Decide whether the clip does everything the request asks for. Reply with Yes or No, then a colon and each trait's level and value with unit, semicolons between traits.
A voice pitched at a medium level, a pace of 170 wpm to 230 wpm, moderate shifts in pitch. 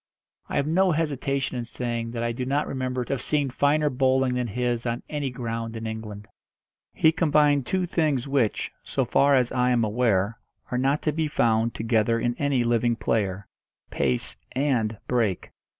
No: low, 125 Hz; average, 180 wpm; average, 3.4 semitones